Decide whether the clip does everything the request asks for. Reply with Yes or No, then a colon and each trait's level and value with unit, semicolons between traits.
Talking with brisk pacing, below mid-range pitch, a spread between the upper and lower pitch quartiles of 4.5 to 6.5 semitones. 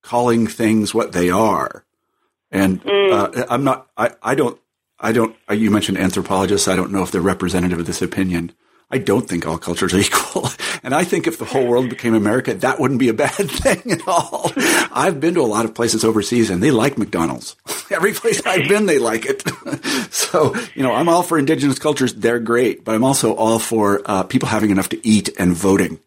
Yes: fast, 210 wpm; low, 110 Hz; average, 4.9 semitones